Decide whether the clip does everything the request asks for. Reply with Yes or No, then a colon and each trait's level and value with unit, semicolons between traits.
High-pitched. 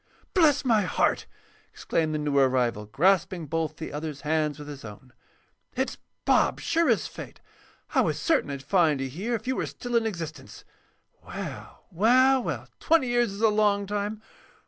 No: medium, 175 Hz